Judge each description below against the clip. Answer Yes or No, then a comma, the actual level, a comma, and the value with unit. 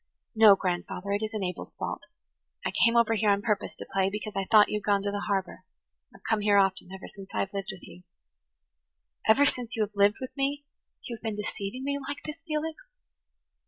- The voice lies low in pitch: No, high, 210 Hz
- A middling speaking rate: No, fast, 220 wpm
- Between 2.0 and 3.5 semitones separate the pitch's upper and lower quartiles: Yes, average, 2.9 semitones